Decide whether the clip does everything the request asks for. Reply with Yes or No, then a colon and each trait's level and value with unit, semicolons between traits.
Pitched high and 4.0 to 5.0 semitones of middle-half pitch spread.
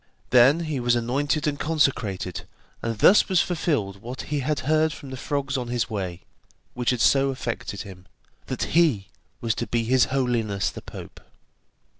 No: low, 125 Hz; average, 4.3 semitones